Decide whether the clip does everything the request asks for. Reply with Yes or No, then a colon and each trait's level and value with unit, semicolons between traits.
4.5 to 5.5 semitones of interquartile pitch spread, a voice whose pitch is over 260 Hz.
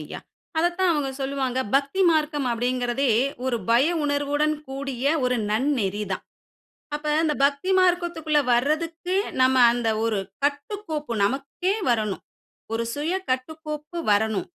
No: average, 3.9 semitones; very high, 280 Hz